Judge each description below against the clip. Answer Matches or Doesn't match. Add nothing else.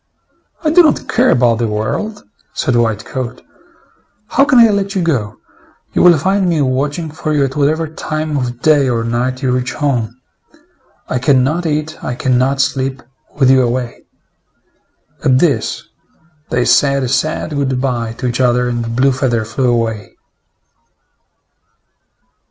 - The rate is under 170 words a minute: Matches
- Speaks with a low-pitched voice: Matches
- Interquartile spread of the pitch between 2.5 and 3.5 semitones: Doesn't match